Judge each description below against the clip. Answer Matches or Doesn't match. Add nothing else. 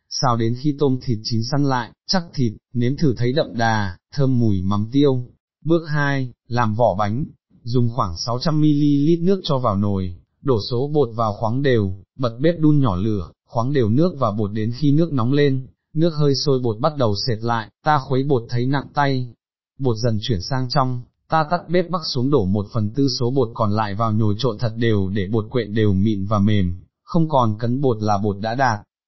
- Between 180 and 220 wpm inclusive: Matches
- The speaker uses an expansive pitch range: Doesn't match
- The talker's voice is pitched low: Matches